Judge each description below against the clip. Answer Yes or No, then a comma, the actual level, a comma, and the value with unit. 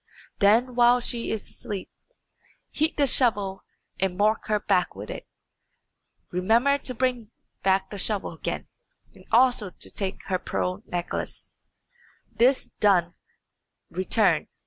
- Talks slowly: Yes, slow, 125 wpm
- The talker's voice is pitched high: Yes, high, 210 Hz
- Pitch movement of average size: Yes, average, 4.3 semitones